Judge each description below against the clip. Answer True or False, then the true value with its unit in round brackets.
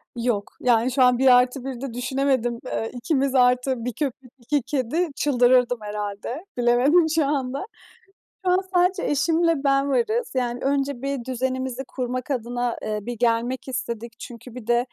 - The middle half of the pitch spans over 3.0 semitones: False (2.4 semitones)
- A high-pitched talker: True (255 Hz)